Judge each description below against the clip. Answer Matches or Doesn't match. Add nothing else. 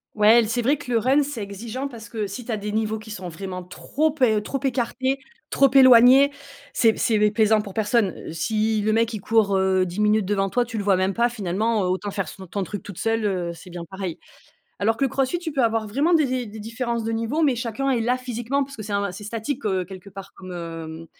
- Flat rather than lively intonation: Doesn't match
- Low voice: Doesn't match